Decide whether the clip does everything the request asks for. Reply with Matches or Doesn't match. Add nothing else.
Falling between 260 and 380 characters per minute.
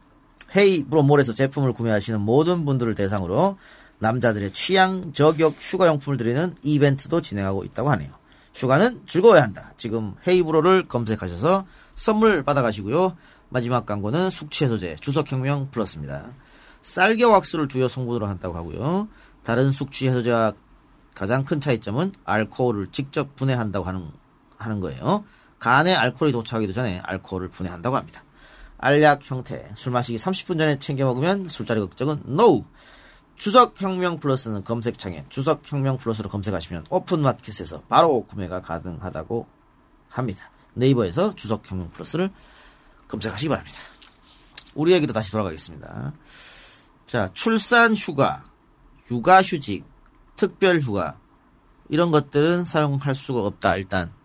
Matches